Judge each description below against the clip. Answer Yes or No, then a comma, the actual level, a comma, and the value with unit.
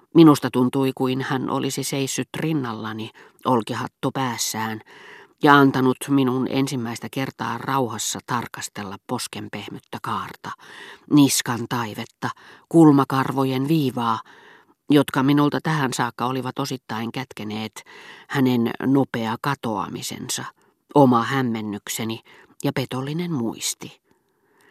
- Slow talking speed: Yes, slow, 90 wpm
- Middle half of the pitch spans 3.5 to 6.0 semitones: No, average, 3.0 semitones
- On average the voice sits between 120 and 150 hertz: Yes, low, 130 Hz